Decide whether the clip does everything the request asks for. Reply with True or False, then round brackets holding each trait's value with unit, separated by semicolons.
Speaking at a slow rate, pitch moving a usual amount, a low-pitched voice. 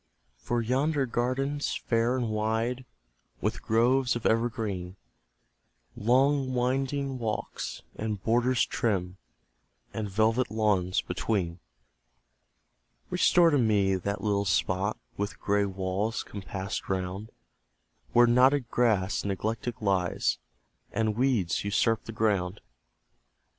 True (105 wpm; 3.8 semitones; 110 Hz)